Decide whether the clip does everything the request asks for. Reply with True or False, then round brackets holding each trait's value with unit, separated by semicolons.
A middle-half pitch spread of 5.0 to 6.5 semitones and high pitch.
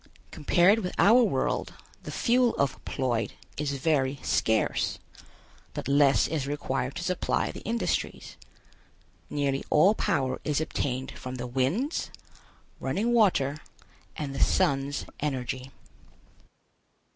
False (5.4 semitones; 140 Hz)